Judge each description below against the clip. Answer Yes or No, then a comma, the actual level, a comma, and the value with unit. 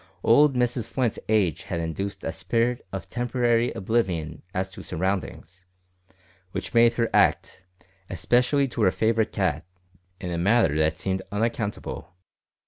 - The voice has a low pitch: Yes, low, 105 Hz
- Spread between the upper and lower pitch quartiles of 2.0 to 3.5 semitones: No, average, 4.6 semitones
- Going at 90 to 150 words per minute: Yes, slow, 135 wpm